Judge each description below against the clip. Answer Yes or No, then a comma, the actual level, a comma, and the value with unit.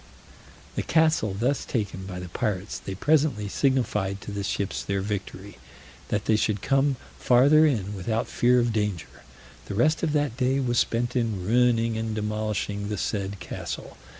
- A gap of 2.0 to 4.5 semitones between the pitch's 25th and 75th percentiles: Yes, average, 3.8 semitones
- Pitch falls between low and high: No, low, 110 Hz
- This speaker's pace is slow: No, average, 165 wpm